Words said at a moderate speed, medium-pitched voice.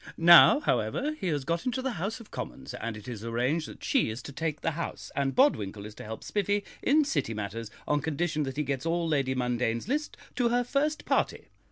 No: fast, 220 wpm; medium, 155 Hz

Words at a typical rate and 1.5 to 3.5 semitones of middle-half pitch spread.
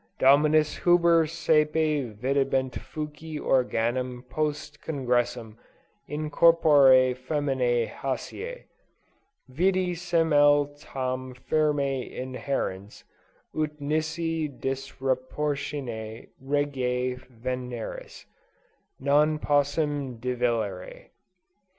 No: slow, 70 wpm; average, 3.1 semitones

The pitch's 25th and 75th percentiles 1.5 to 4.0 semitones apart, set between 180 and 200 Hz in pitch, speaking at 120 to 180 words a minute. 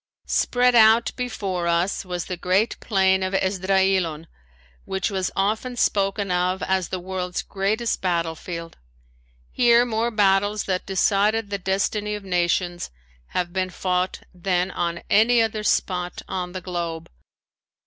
Yes: average, 2.7 semitones; high, 190 Hz; slow, 135 wpm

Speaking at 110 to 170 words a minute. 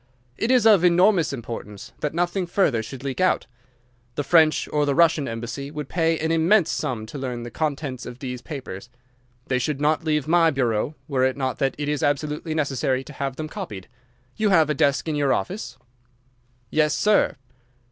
No: average, 190 wpm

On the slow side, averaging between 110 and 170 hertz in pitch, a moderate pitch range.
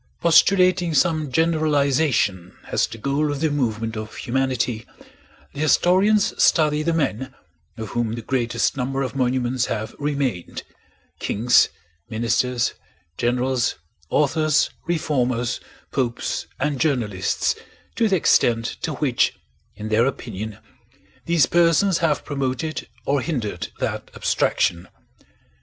Yes: slow, 115 wpm; low, 135 Hz; average, 4.8 semitones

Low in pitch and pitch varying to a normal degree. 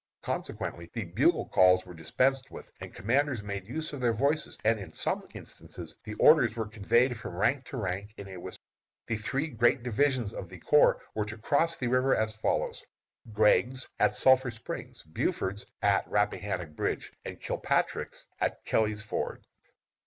Yes: low, 110 Hz; average, 4.6 semitones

